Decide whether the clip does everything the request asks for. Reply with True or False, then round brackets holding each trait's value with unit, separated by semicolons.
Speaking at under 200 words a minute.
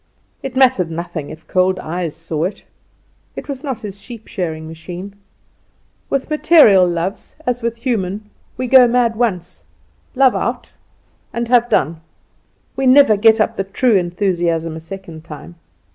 True (150 wpm)